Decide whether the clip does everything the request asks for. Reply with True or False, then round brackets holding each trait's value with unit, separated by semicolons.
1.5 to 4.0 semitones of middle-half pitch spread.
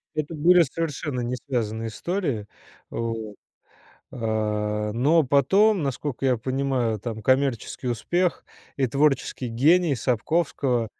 False (4.8 semitones)